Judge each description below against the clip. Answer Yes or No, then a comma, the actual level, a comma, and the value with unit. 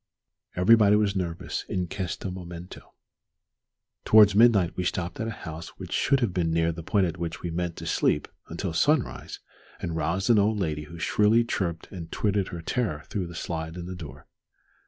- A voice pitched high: No, very low, 90 Hz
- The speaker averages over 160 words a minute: Yes, average, 185 wpm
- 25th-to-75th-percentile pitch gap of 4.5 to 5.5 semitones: No, average, 3.7 semitones